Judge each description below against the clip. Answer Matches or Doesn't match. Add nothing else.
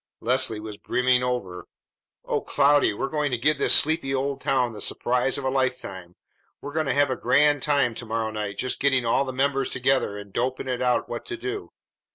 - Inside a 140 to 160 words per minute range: Doesn't match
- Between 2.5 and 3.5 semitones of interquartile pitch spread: Matches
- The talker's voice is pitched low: Matches